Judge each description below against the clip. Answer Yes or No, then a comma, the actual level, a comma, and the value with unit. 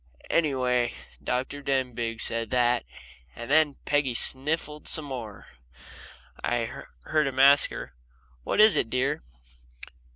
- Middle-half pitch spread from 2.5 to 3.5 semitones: Yes, average, 3.2 semitones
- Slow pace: Yes, slow, 125 wpm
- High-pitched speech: No, low, 130 Hz